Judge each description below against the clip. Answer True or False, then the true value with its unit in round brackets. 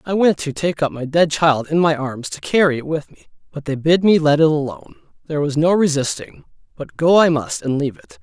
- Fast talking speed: True (250 wpm)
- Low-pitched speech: False (155 Hz)